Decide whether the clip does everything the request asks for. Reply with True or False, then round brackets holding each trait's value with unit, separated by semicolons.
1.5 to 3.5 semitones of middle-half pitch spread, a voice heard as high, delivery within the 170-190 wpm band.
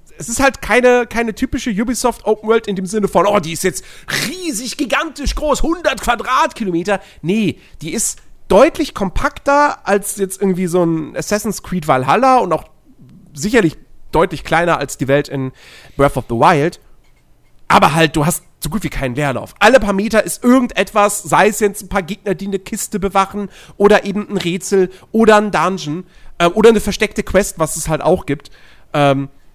False (5.5 semitones; 200 Hz; 185 wpm)